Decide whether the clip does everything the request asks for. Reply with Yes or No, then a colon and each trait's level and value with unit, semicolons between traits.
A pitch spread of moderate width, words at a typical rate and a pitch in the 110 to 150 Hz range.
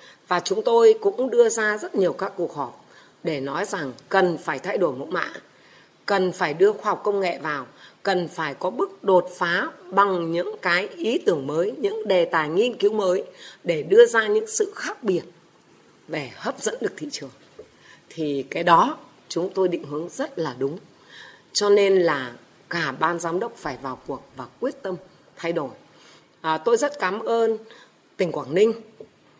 No: average, 5.0 semitones; average, 185 wpm; high, 190 Hz